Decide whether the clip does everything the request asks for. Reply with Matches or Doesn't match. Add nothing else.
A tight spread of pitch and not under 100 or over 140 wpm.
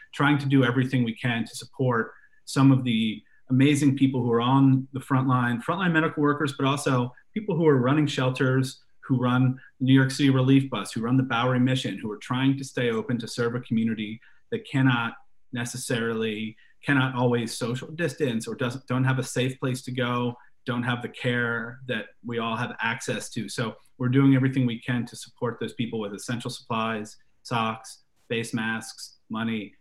Doesn't match